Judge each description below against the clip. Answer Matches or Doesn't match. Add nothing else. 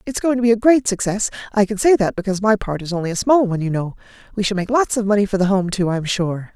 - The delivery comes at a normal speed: Doesn't match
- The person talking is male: Doesn't match